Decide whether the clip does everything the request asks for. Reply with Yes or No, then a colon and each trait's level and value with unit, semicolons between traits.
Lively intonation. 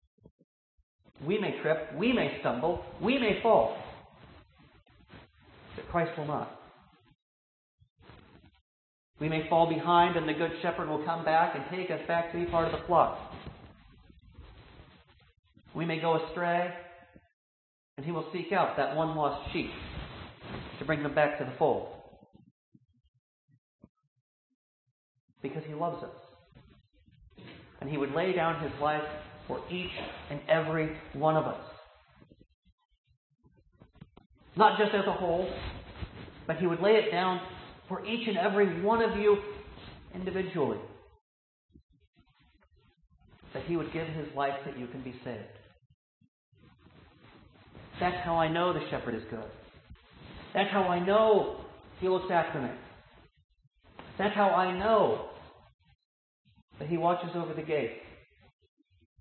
Yes: wide, 6.1 semitones